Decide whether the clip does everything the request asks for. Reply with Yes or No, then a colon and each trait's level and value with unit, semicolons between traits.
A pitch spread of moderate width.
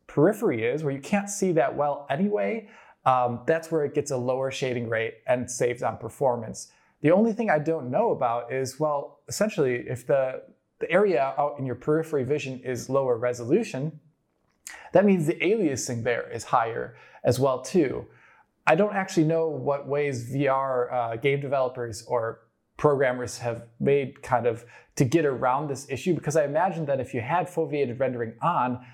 Yes: average, 4.1 semitones